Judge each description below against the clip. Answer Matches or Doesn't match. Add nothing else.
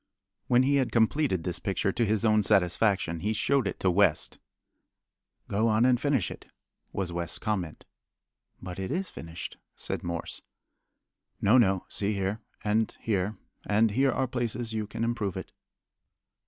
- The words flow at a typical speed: Matches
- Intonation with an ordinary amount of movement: Matches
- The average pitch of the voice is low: Matches